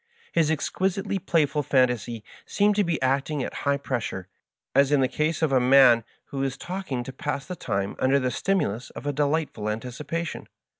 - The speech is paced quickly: No, average, 180 wpm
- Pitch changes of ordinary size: Yes, average, 4.0 semitones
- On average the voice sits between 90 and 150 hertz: Yes, medium, 140 Hz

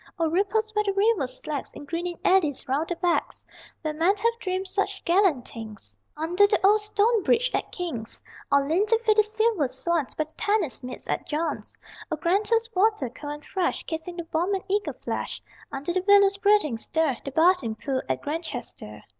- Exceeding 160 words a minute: Yes, average, 190 wpm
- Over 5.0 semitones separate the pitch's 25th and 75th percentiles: Yes, wide, 5.6 semitones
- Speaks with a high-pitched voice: Yes, very high, 345 Hz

